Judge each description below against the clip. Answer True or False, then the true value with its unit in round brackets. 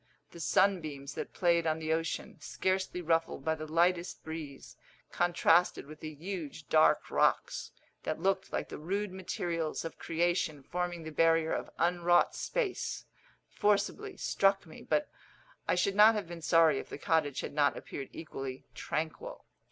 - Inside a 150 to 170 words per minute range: True (155 wpm)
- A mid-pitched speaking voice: True (165 Hz)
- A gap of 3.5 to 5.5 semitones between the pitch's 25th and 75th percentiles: False (2.6 semitones)